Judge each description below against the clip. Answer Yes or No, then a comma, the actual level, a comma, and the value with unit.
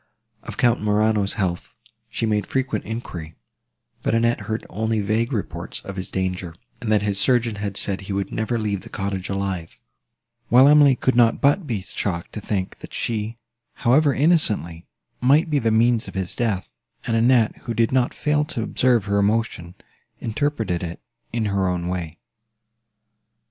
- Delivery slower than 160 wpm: No, average, 170 wpm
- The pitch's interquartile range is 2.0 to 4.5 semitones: Yes, average, 3.6 semitones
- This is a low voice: Yes, low, 110 Hz